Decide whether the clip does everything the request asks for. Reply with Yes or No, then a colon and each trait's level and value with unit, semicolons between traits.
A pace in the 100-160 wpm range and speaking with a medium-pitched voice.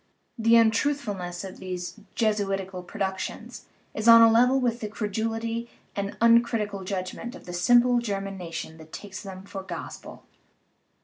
No: average, 150 wpm; high, 210 Hz